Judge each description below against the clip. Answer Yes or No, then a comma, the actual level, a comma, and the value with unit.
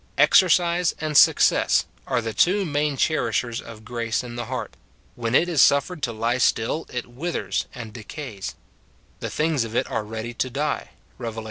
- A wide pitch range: No, average, 4.8 semitones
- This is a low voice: Yes, low, 125 Hz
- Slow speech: No, average, 175 wpm